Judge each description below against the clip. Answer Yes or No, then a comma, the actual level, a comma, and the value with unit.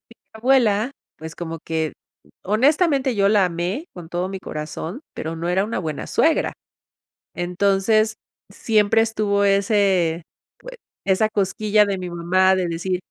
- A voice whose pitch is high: Yes, high, 195 Hz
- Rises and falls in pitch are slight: No, average, 3.7 semitones